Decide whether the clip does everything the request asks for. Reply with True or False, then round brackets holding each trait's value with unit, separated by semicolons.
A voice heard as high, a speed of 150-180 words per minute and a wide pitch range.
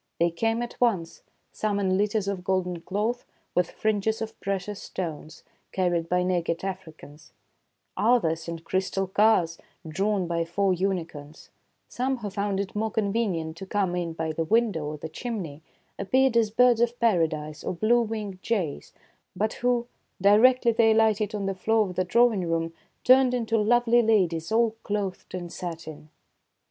False (195 Hz; 160 wpm; 4.7 semitones)